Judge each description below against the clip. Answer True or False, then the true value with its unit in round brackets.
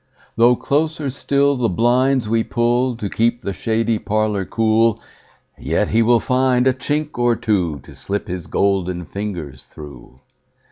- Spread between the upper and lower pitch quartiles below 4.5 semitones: True (4.1 semitones)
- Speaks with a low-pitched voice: True (115 Hz)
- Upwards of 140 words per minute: False (135 wpm)